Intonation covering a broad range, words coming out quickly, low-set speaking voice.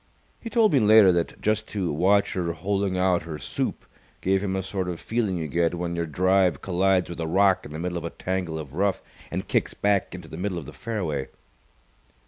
No: average, 2.8 semitones; fast, 220 wpm; very low, 90 Hz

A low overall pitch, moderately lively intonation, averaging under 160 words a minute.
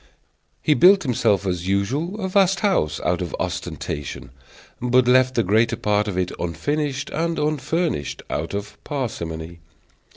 No: low, 120 Hz; wide, 8.8 semitones; average, 140 wpm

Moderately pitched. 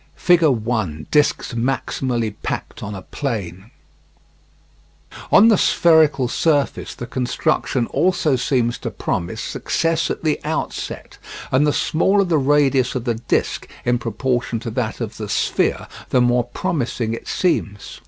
No: low, 125 Hz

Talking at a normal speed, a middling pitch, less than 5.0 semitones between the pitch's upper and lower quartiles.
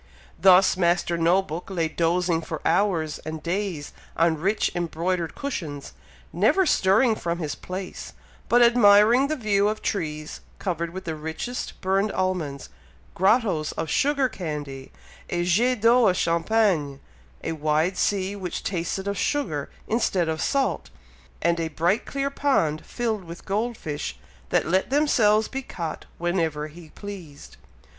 Yes: average, 145 wpm; medium, 180 Hz; average, 4.6 semitones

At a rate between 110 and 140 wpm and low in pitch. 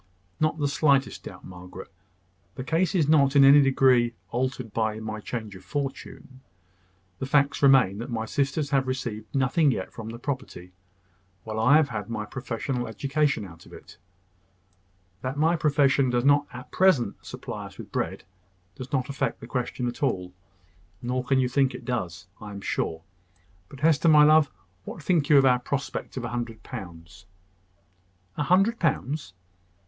No: average, 175 wpm; low, 130 Hz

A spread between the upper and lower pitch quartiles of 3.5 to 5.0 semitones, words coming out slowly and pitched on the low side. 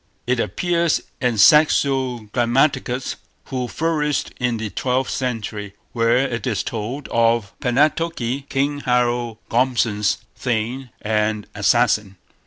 No: average, 3.1 semitones; slow, 110 wpm; low, 125 Hz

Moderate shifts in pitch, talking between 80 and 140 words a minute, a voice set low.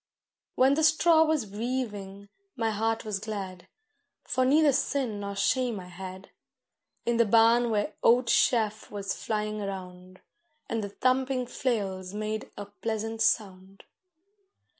No: average, 3.9 semitones; slow, 135 wpm; high, 215 Hz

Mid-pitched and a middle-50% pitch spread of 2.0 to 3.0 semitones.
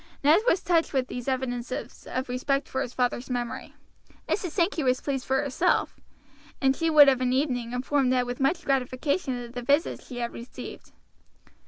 No: very high, 260 Hz; narrow, 2.6 semitones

